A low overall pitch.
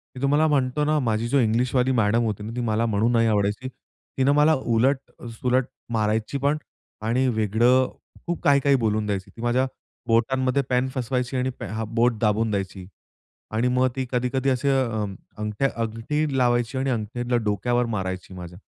Yes: low, 120 Hz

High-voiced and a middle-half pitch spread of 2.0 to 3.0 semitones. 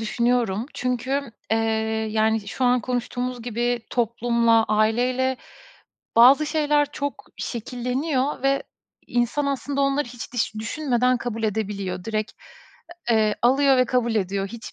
Yes: high, 245 Hz; average, 2.7 semitones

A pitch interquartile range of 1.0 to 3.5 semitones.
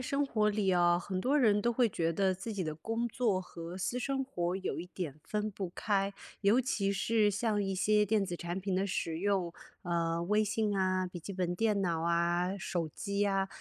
Yes: average, 3.1 semitones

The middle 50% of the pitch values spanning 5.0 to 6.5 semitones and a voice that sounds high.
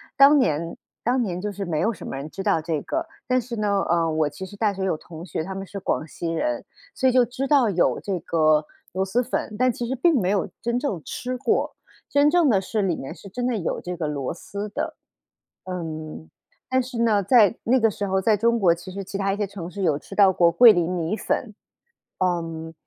Yes: wide, 5.6 semitones; high, 195 Hz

